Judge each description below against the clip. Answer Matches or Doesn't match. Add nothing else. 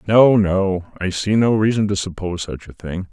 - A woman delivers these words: Doesn't match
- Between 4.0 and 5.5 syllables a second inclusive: Matches